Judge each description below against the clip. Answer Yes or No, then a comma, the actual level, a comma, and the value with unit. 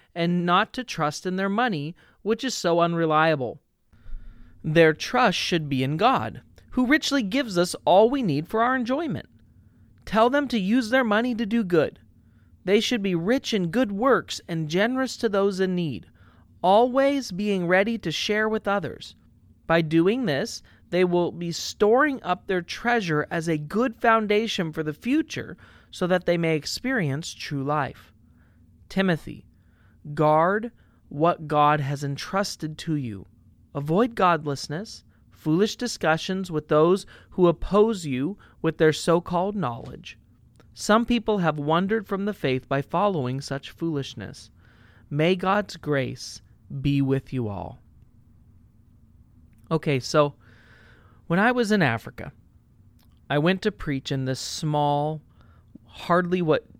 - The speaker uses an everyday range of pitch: No, wide, 7.0 semitones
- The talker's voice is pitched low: No, medium, 165 Hz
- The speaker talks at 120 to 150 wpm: Yes, average, 145 wpm